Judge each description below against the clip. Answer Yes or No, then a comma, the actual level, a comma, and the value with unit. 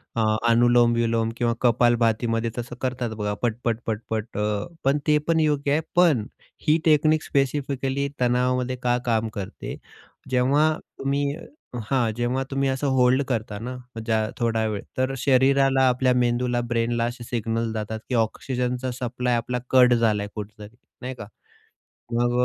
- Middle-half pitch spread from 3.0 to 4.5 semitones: No, narrow, 2.4 semitones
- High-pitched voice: No, low, 125 Hz